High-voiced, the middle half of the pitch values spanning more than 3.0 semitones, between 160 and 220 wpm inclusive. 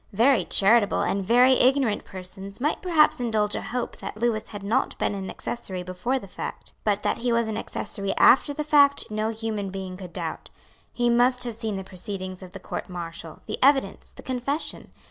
Yes: high, 215 Hz; average, 4.4 semitones; average, 195 wpm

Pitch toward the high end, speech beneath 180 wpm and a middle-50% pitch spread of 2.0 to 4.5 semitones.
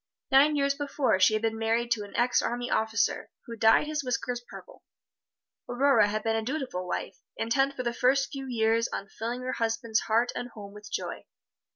No: high, 235 Hz; average, 195 wpm; average, 3.2 semitones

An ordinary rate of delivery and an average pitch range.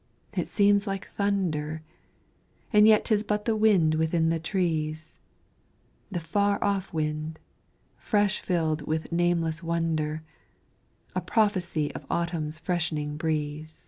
No: slow, 120 wpm; average, 4.3 semitones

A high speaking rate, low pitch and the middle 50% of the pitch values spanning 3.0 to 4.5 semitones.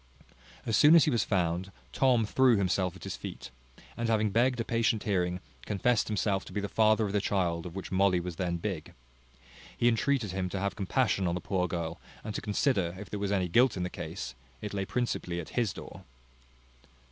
Yes: fast, 210 wpm; low, 100 Hz; average, 3.8 semitones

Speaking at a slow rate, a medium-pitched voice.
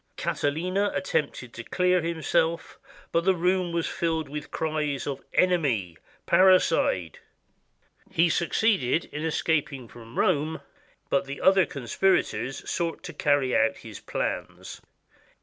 Yes: slow, 130 wpm; medium, 160 Hz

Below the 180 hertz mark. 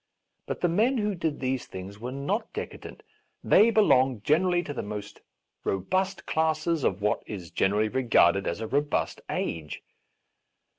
Yes: low, 135 Hz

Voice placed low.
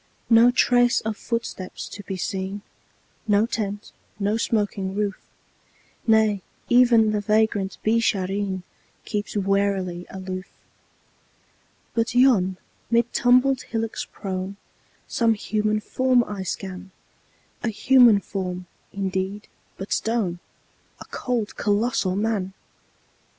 No: high, 205 Hz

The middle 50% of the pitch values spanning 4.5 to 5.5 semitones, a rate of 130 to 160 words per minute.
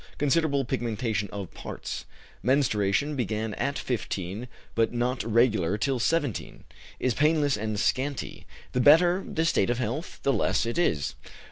Yes: average, 4.8 semitones; average, 140 wpm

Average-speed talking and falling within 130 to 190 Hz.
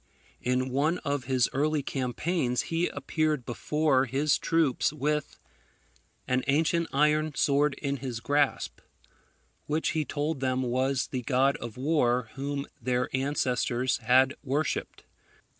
No: slow, 125 wpm; medium, 140 Hz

